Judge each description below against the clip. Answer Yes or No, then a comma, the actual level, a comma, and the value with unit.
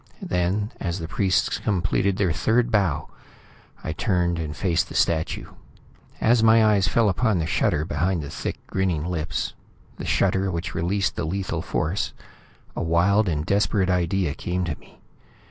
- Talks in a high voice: No, very low, 90 Hz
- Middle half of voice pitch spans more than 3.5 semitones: No, average, 3.2 semitones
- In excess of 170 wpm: No, average, 160 wpm